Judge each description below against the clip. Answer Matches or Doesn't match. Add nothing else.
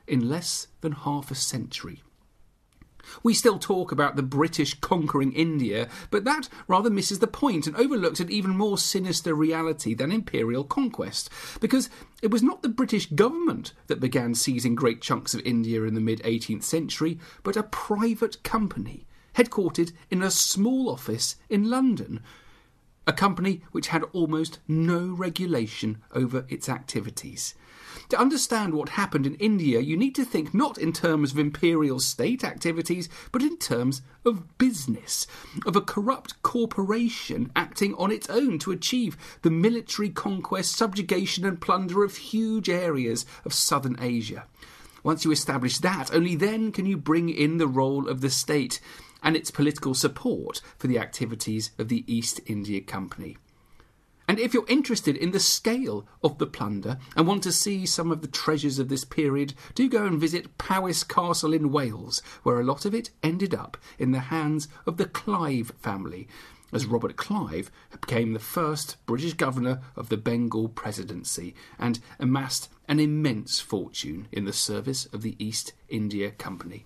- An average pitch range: Doesn't match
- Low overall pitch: Doesn't match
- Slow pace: Doesn't match